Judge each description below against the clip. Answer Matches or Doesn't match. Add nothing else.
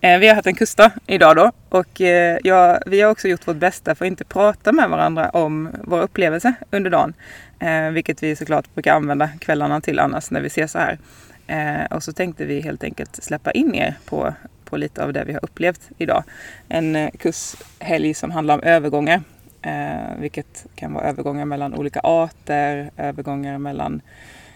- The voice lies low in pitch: Doesn't match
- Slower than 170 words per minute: Doesn't match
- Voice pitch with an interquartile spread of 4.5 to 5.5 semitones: Doesn't match